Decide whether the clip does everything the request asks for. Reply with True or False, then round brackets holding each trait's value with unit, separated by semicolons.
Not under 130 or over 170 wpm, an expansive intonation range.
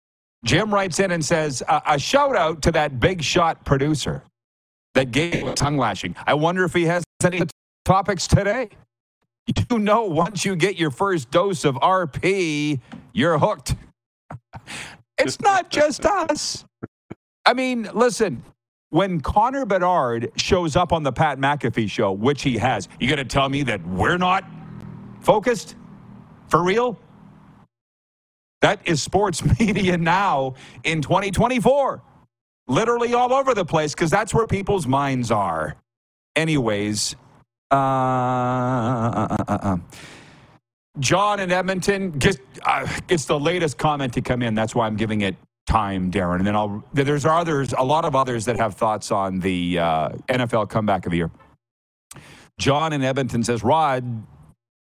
True (150 wpm; 7.2 semitones)